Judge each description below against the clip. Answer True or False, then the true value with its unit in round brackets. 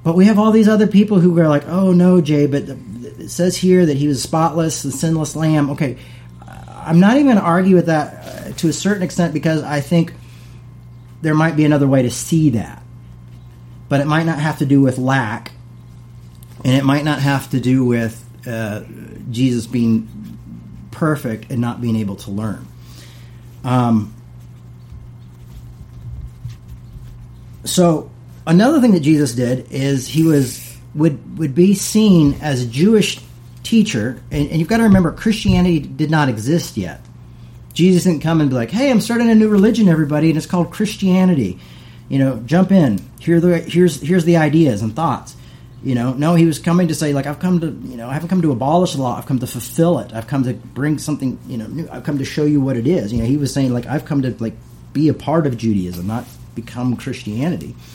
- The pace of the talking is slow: False (205 wpm)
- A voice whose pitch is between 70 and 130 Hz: False (140 Hz)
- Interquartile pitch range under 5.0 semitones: False (5.6 semitones)